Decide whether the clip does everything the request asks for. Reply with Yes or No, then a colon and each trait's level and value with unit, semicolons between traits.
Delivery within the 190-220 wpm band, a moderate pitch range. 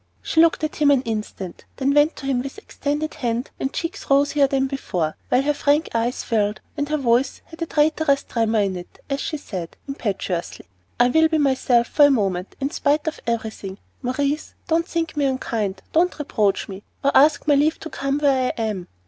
Yes: average, 200 wpm; average, 4.7 semitones